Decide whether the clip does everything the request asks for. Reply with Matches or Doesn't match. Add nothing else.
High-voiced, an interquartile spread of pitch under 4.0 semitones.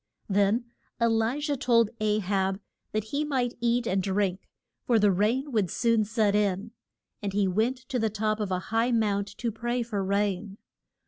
Matches